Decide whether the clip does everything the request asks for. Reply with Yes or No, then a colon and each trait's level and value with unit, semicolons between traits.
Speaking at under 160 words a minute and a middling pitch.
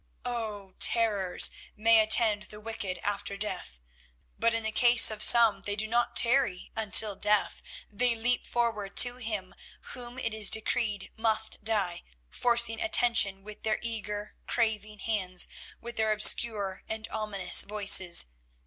No: average, 140 wpm; high, 215 Hz